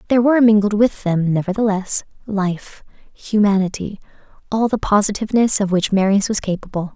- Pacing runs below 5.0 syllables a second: No, 5.5 syllables/s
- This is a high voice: Yes, high, 205 Hz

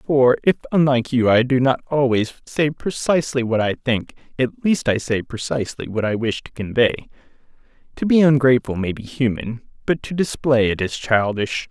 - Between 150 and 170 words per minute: No, average, 180 wpm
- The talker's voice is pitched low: Yes, low, 125 Hz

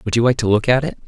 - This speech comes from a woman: No, male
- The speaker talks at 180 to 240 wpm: No, fast, 390 wpm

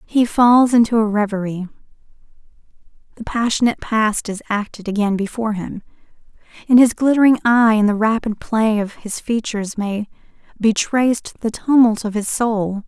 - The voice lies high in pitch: Yes, high, 220 Hz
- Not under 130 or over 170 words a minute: Yes, average, 150 wpm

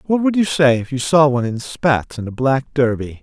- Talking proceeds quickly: Yes, fast, 260 wpm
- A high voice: No, low, 135 Hz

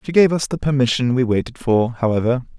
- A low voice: Yes, low, 130 Hz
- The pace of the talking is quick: Yes, fast, 210 wpm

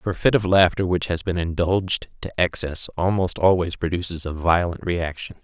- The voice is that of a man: Yes, male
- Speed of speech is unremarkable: Yes, average, 190 wpm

